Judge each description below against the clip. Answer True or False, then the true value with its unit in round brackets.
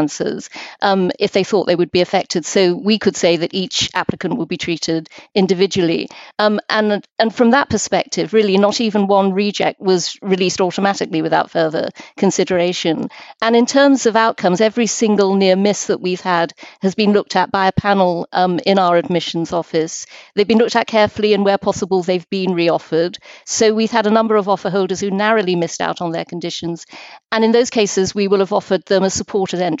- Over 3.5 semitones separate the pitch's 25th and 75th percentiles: False (2.9 semitones)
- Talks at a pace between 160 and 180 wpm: False (200 wpm)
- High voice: True (195 Hz)